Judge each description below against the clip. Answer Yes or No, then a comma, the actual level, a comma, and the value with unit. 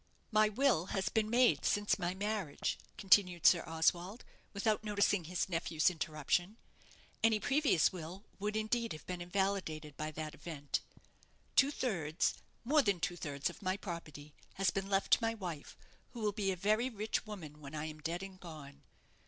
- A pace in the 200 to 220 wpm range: No, average, 170 wpm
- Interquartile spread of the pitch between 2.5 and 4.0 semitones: No, average, 4.9 semitones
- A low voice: No, high, 190 Hz